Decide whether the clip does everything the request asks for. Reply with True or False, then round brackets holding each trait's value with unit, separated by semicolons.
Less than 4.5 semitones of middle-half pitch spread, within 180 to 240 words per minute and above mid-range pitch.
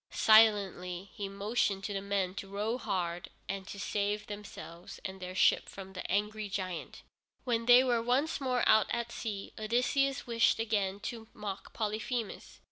False (2.9 semitones; 155 wpm; 210 Hz)